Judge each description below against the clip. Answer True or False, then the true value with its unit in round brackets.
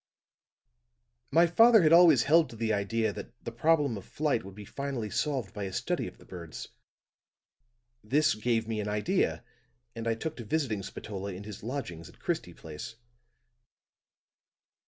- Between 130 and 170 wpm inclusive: True (160 wpm)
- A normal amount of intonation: False (6.2 semitones)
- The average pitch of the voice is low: True (115 Hz)